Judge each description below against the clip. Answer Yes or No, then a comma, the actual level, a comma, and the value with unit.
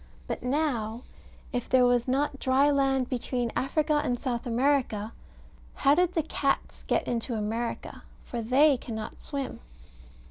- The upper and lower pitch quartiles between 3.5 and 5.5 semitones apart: No, average, 2.9 semitones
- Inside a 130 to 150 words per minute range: Yes, average, 140 wpm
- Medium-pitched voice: No, very high, 255 Hz